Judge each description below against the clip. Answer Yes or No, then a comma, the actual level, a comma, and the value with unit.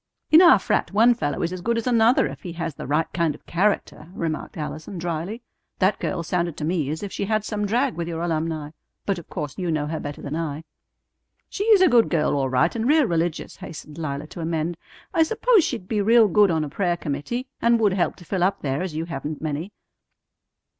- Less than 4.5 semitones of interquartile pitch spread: No, wide, 5.5 semitones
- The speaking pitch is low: No, medium, 175 Hz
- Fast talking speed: Yes, fast, 230 wpm